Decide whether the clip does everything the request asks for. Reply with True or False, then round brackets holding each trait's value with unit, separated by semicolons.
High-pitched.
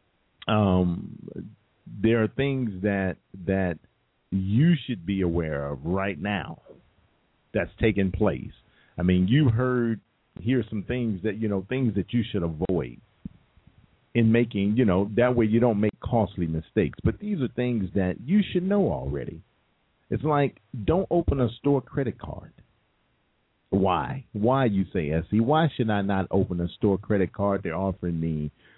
False (105 Hz)